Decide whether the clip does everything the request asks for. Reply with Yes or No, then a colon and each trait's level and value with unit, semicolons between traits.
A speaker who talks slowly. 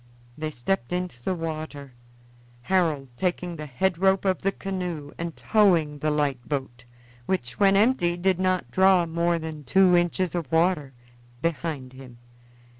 No: average, 150 wpm